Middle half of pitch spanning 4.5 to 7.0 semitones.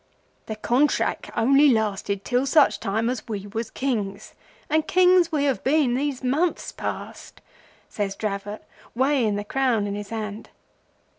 Yes: average, 5.1 semitones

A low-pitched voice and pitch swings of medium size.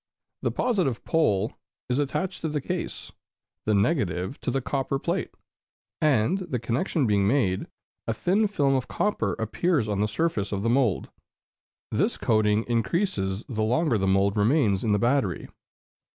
No: low, 120 Hz; wide, 6.6 semitones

